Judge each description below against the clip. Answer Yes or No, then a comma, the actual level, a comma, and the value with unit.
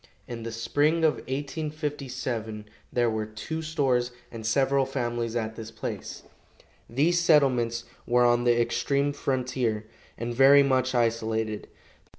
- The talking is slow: Yes, slow, 130 wpm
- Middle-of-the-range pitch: No, low, 125 Hz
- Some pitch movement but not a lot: Yes, average, 3.3 semitones